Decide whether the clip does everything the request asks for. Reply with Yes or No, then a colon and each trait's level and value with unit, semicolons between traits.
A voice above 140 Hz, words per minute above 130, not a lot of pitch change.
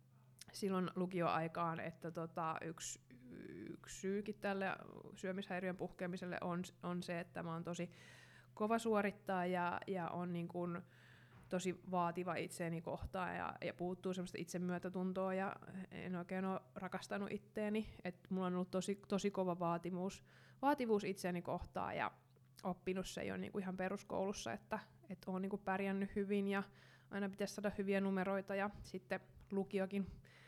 Yes: medium, 185 Hz; average, 140 wpm; narrow, 2.1 semitones